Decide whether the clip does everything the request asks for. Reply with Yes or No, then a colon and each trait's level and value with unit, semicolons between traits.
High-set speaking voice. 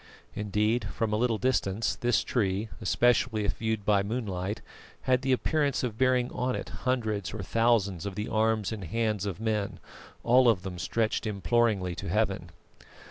No: low, 110 Hz